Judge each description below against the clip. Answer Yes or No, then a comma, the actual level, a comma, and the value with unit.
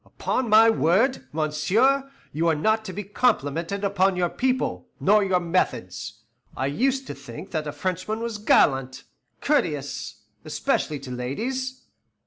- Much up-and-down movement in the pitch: Yes, wide, 7.2 semitones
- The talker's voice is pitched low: No, medium, 185 Hz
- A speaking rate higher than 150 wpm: No, average, 140 wpm